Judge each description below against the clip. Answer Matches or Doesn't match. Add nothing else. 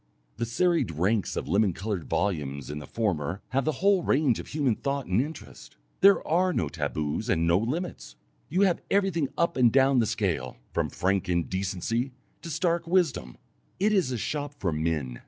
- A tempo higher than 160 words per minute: Matches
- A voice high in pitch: Doesn't match